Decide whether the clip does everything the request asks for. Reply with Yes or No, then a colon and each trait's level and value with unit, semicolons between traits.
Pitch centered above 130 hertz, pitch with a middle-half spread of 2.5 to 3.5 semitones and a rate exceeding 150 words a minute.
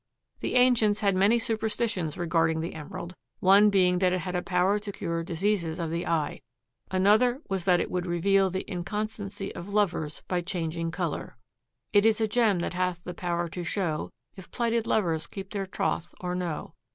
Yes: medium, 185 Hz; average, 3.1 semitones; average, 185 wpm